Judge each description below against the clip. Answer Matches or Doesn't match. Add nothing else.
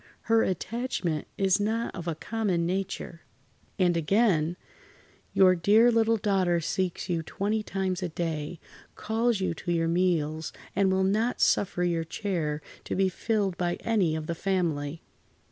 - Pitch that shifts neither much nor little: Matches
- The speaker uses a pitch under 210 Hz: Matches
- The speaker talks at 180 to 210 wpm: Doesn't match